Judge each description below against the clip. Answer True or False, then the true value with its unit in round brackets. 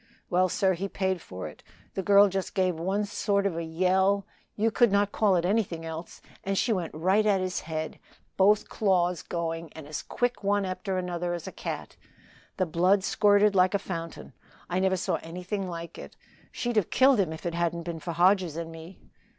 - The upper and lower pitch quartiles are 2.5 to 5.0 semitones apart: True (2.9 semitones)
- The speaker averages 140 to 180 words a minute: False (200 wpm)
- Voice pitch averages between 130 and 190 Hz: True (185 Hz)